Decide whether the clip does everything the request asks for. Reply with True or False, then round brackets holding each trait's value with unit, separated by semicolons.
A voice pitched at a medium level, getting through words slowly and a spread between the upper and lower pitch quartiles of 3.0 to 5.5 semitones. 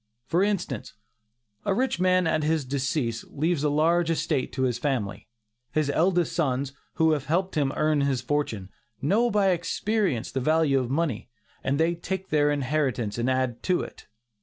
False (150 Hz; 170 wpm; 4.5 semitones)